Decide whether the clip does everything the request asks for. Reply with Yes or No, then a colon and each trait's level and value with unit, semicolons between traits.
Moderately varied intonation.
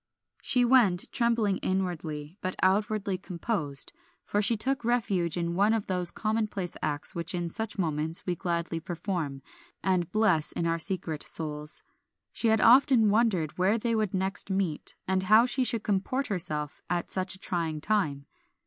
Yes: average, 4.3 semitones